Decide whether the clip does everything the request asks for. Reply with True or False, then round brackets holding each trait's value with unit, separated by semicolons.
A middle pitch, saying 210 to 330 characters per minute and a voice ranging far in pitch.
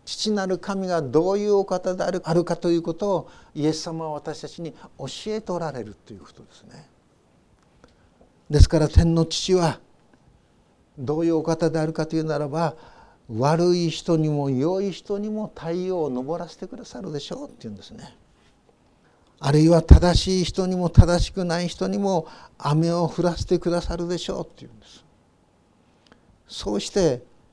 False (165 Hz; 310 characters per minute; 2.7 semitones)